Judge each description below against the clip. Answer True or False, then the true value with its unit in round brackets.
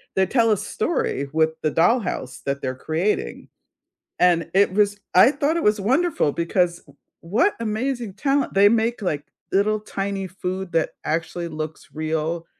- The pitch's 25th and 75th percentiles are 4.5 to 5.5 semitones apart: True (4.9 semitones)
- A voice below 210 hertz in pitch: True (190 Hz)